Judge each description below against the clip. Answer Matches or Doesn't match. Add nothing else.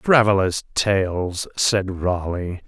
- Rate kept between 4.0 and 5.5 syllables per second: Doesn't match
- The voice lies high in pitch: Doesn't match